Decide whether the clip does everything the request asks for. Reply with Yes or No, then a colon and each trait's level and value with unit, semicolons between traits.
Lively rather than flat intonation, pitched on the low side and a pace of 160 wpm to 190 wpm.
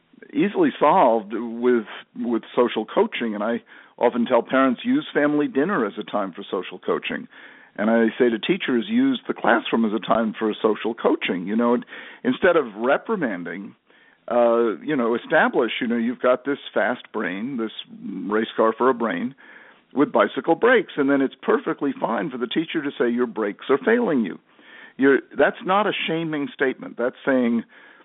Yes: wide, 7.2 semitones; low, 125 Hz; average, 180 wpm